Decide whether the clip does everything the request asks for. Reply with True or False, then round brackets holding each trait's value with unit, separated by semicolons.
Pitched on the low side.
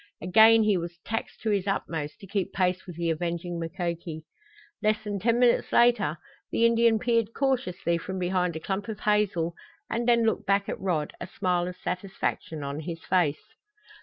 False (190 Hz)